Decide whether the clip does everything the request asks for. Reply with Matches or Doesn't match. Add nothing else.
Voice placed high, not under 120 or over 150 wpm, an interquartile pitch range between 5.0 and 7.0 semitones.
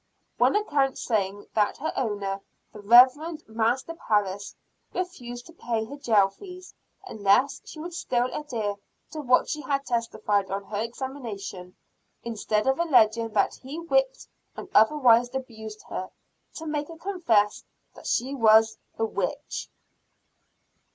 Matches